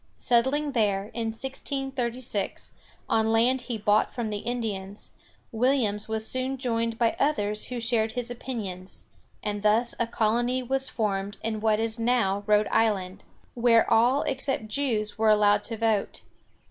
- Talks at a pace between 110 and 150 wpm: Yes, average, 145 wpm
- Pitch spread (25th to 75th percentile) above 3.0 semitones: No, average, 2.7 semitones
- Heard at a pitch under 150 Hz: No, high, 225 Hz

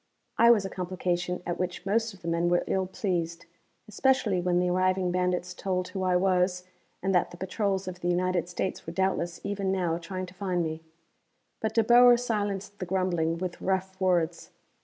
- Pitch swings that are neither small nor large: No, narrow, 1.5 semitones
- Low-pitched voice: No, medium, 185 Hz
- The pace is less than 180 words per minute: No, average, 190 wpm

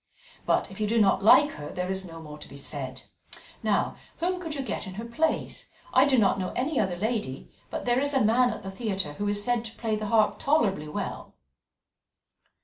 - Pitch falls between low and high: No, high, 215 Hz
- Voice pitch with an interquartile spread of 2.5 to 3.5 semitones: No, average, 4.6 semitones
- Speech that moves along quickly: Yes, fast, 220 wpm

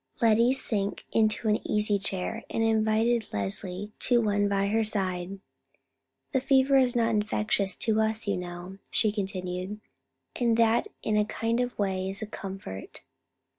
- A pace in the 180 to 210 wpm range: No, average, 155 wpm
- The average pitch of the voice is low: No, high, 210 Hz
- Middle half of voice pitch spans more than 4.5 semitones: No, average, 2.7 semitones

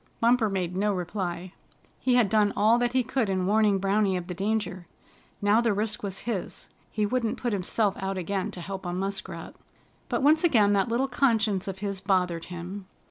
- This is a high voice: Yes, high, 200 Hz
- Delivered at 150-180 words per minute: No, average, 190 wpm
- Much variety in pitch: No, average, 2.9 semitones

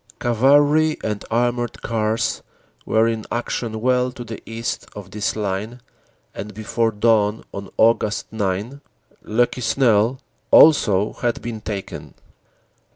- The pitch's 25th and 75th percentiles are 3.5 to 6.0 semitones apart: No, narrow, 2.4 semitones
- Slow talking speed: Yes, slow, 120 wpm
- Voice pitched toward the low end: Yes, low, 115 Hz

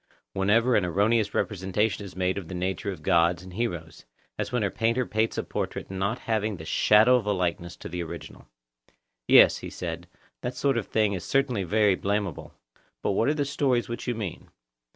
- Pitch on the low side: Yes, low, 105 Hz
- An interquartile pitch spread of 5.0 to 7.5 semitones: No, average, 4.0 semitones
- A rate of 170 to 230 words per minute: Yes, average, 195 wpm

